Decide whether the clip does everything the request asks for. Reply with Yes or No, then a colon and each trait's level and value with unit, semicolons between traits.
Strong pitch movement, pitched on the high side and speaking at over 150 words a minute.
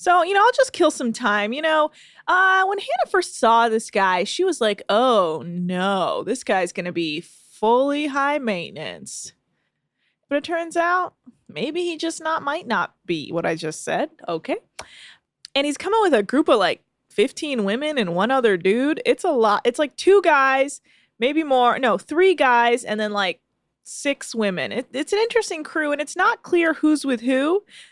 Yes: wide, 7.9 semitones; very high, 280 Hz; average, 190 wpm